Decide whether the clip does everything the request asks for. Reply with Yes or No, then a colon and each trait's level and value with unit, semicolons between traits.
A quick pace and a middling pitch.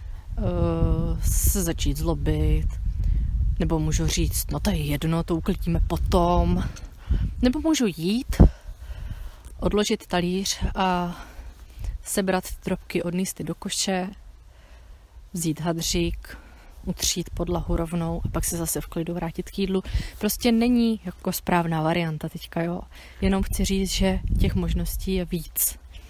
No: average, 130 wpm; medium, 170 Hz